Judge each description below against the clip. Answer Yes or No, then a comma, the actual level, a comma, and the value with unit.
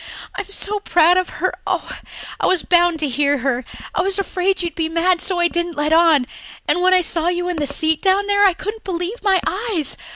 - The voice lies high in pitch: Yes, very high, 350 Hz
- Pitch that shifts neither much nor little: Yes, average, 3.0 semitones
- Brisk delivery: Yes, fast, 225 wpm